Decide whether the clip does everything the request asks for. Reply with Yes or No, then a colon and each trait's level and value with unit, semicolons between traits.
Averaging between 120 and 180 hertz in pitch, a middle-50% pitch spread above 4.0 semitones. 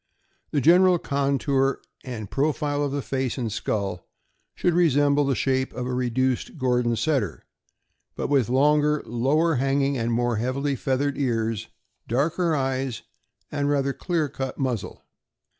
No: low, 135 Hz; average, 2.8 semitones